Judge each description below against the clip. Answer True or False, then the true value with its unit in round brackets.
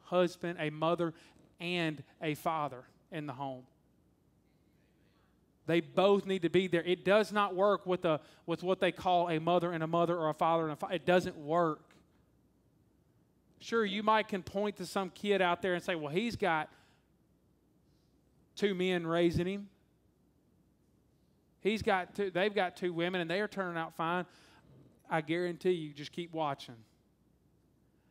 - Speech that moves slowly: False (165 wpm)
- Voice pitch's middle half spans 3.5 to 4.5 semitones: False (2.8 semitones)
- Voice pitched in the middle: True (175 Hz)